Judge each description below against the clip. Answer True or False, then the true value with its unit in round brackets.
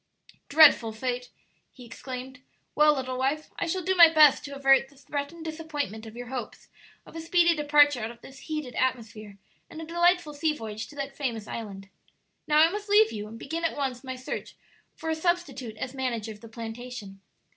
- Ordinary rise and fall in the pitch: True (5.0 semitones)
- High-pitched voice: True (270 Hz)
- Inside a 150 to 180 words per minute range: False (195 wpm)